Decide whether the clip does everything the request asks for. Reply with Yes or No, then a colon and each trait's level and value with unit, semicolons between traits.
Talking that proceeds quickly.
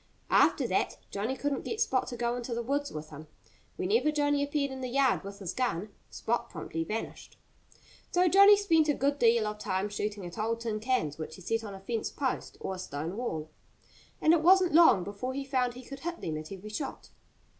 Yes: fast, 215 wpm